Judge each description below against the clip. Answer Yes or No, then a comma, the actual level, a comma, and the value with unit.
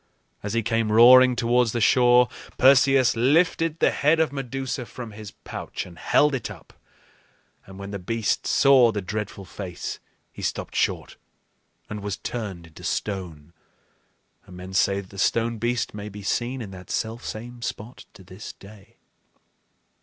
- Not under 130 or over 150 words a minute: No, average, 160 wpm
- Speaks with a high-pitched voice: No, low, 115 Hz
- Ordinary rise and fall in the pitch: Yes, average, 3.9 semitones